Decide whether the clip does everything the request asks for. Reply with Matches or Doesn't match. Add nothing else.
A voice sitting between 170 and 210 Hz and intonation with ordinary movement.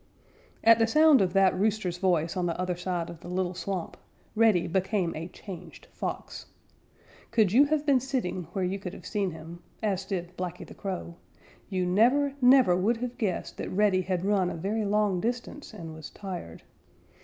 Matches